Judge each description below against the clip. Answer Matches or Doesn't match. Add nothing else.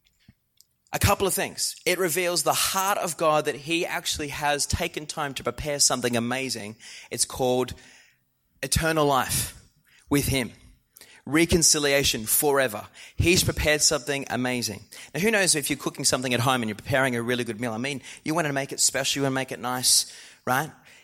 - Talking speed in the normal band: Matches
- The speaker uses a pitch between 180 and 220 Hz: Doesn't match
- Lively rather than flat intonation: Doesn't match